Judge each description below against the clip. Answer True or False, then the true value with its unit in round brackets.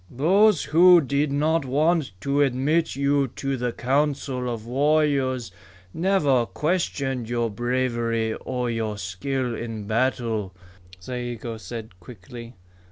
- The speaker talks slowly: True (115 wpm)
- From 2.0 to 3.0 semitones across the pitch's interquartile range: False (3.6 semitones)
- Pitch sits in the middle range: False (130 Hz)